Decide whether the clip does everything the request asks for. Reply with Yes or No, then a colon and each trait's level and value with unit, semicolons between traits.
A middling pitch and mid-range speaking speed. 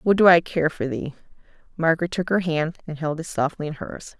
No: medium, 160 Hz; fast, 230 wpm